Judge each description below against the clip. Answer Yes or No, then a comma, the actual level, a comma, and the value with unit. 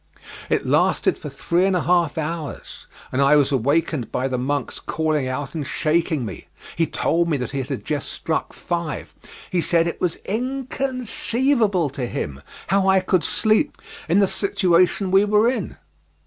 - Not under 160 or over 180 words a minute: Yes, average, 170 wpm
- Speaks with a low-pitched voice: No, medium, 170 Hz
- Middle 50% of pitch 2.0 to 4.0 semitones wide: No, average, 5.2 semitones